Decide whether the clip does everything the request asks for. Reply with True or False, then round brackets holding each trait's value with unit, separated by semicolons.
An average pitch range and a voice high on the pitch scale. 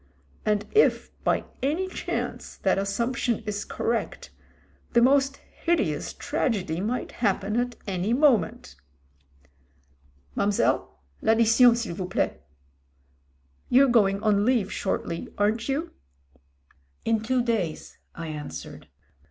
True (4.1 semitones; 225 Hz)